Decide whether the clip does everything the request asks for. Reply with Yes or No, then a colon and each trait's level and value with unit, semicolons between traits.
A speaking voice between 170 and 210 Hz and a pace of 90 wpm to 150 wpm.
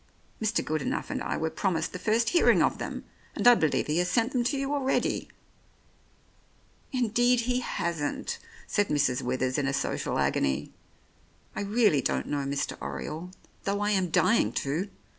No: high, 190 Hz; average, 170 wpm